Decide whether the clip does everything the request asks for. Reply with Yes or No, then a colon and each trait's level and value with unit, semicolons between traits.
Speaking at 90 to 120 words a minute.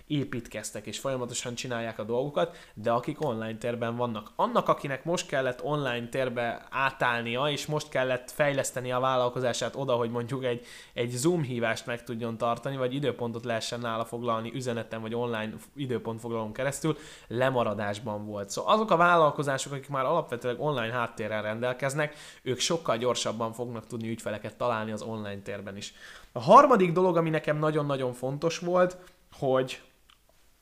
No: average, 150 wpm